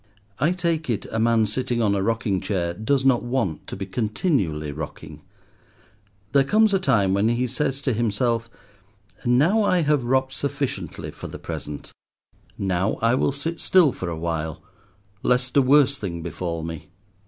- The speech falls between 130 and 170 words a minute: Yes, average, 165 wpm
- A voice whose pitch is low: Yes, low, 115 Hz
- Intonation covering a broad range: Yes, wide, 6.3 semitones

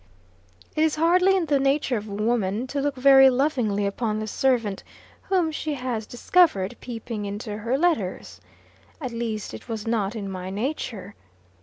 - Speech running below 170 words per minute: Yes, average, 160 wpm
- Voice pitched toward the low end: No, high, 240 Hz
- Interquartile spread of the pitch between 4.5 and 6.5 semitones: Yes, average, 5.1 semitones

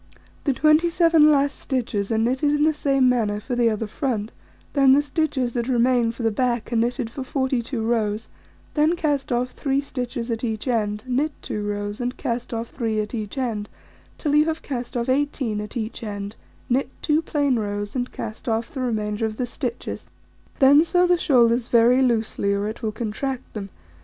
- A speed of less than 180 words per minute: No, average, 190 wpm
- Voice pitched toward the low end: No, high, 245 Hz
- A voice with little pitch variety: No, average, 3.8 semitones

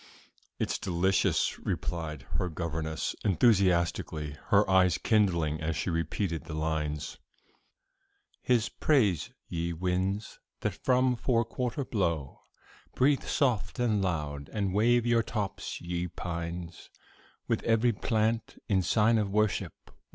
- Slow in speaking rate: Yes, slow, 120 wpm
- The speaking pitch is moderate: No, very low, 95 Hz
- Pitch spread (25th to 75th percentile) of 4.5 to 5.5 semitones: Yes, average, 5.1 semitones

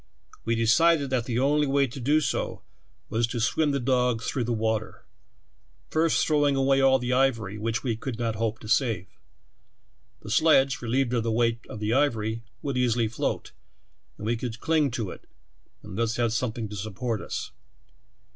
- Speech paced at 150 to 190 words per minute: Yes, average, 180 wpm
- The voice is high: No, low, 120 Hz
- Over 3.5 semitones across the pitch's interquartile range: No, average, 3.2 semitones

